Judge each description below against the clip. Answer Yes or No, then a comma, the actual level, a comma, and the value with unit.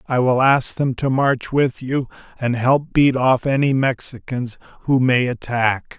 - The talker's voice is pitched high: No, low, 130 Hz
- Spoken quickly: No, average, 170 wpm